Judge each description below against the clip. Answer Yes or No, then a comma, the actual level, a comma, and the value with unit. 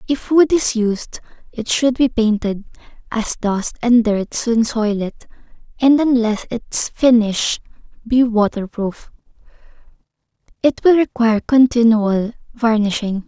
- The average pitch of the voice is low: No, high, 230 Hz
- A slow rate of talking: Yes, slow, 120 wpm